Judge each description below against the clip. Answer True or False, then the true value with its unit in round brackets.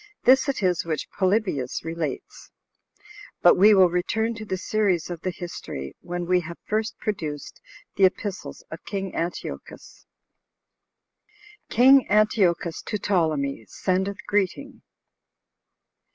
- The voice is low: False (185 Hz)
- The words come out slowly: True (120 wpm)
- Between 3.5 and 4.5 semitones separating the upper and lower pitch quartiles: True (3.8 semitones)